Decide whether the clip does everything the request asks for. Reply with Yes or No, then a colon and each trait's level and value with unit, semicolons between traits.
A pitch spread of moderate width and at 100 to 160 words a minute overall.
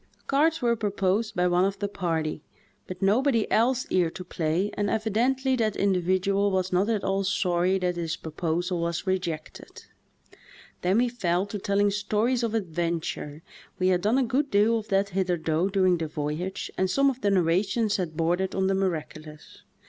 No: average, 3.4 semitones; average, 180 wpm